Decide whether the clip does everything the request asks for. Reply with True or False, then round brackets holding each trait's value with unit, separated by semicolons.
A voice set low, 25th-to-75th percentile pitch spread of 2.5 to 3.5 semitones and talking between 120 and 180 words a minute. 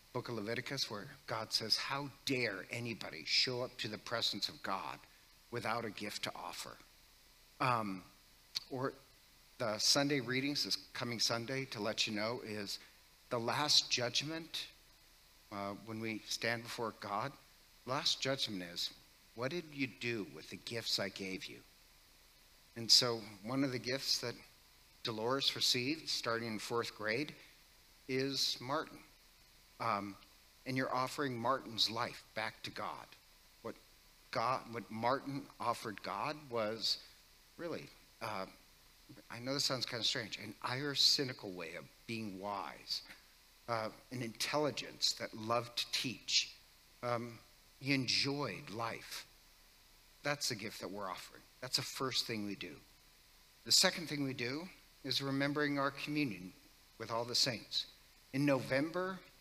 False (120 Hz; 3.9 semitones; 140 wpm)